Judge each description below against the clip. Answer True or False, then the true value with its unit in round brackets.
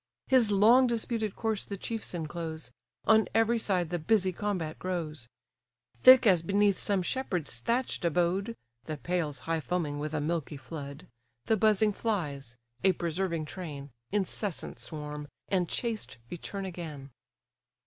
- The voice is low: False (180 Hz)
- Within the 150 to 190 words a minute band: False (140 wpm)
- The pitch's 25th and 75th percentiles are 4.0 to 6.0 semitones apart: True (5.1 semitones)